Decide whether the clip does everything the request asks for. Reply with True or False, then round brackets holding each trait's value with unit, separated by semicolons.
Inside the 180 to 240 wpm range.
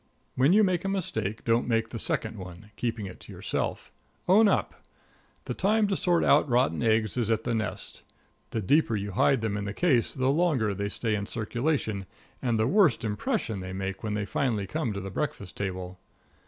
True (200 wpm)